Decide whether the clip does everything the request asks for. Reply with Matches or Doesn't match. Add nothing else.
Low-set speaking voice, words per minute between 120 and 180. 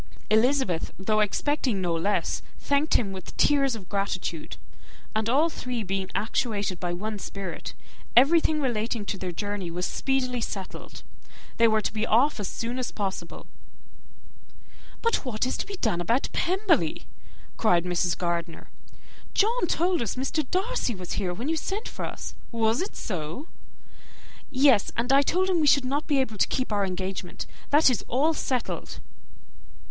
Doesn't match